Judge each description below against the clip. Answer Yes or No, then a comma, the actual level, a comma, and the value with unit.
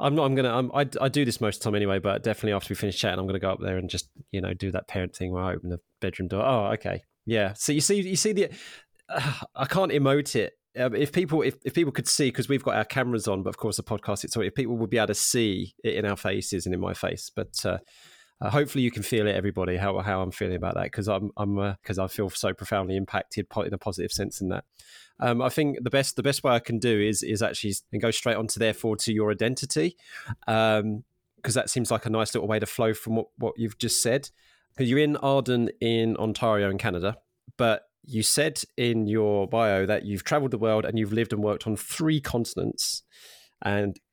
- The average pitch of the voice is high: No, low, 110 Hz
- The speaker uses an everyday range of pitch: Yes, average, 4.2 semitones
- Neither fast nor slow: No, fast, 255 wpm